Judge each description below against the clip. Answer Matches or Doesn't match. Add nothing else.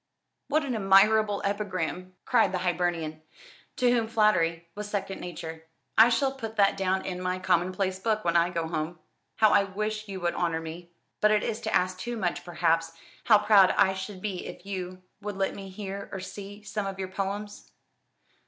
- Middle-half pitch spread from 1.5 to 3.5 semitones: Matches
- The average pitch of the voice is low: Doesn't match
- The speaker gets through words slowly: Doesn't match